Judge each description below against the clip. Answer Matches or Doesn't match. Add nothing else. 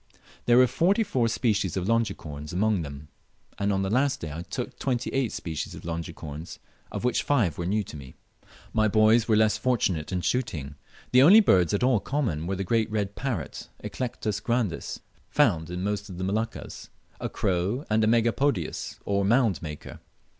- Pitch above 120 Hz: Doesn't match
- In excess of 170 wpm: Matches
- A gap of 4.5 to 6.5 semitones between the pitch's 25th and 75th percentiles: Matches